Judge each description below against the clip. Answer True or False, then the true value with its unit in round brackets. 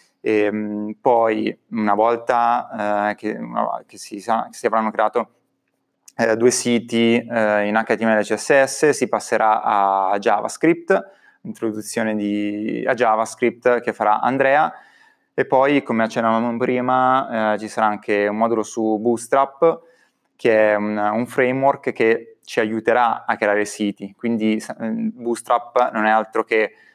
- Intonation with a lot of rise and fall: False (2.7 semitones)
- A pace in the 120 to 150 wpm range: True (135 wpm)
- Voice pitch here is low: True (115 Hz)